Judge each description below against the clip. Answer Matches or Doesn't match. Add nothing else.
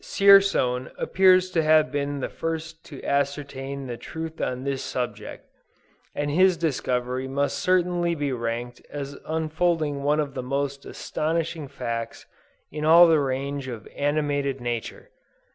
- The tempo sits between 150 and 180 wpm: Doesn't match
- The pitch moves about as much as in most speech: Matches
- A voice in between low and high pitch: Matches